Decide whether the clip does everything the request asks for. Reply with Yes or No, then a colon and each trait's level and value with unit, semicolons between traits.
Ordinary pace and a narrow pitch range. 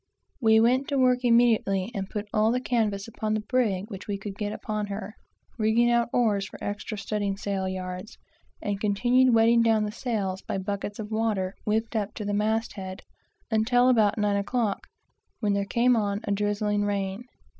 Yes: average, 180 wpm; narrow, 2.3 semitones